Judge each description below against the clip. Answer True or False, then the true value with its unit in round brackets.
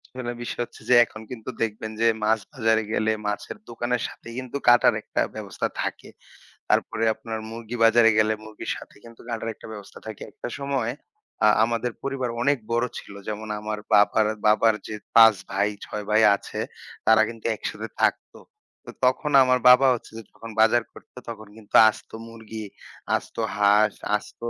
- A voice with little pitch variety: True (1.8 semitones)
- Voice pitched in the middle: False (115 Hz)